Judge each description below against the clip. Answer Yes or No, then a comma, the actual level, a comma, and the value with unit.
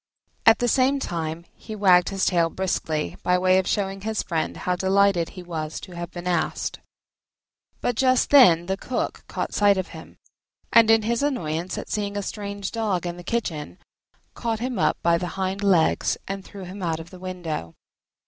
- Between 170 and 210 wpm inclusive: Yes, average, 190 wpm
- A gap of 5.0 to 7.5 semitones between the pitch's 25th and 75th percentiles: No, average, 3.3 semitones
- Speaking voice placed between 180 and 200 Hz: Yes, high, 190 Hz